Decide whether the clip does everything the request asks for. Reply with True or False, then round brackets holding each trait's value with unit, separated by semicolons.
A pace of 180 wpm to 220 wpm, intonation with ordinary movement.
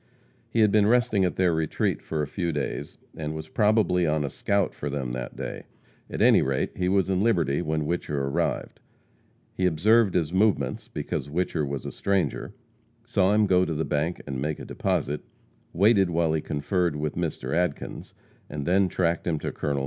True (190 wpm; 4.2 semitones)